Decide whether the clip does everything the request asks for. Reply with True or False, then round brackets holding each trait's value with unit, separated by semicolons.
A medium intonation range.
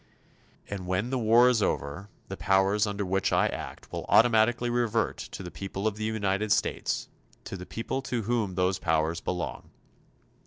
True (3.2 semitones)